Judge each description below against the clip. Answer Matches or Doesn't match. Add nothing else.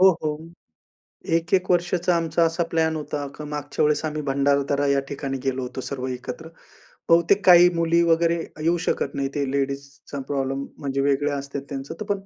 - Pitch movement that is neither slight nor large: Matches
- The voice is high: Doesn't match